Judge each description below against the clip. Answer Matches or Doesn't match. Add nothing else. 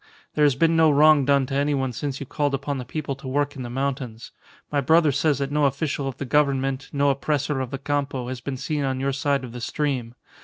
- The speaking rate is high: Matches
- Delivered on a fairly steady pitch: Matches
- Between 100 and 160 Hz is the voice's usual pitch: Matches